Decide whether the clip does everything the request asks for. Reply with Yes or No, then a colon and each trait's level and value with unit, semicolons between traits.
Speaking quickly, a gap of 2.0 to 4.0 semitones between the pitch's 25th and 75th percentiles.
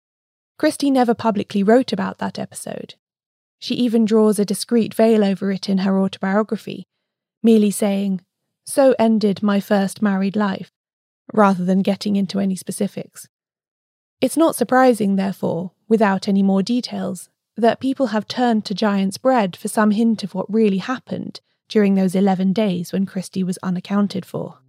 No: average, 155 wpm; narrow, 2.5 semitones